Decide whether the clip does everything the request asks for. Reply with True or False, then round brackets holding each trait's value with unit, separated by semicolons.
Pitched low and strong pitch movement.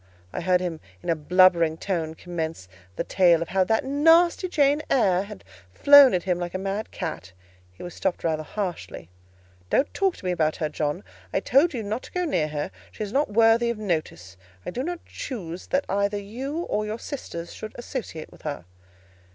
False (190 Hz; 7.0 semitones)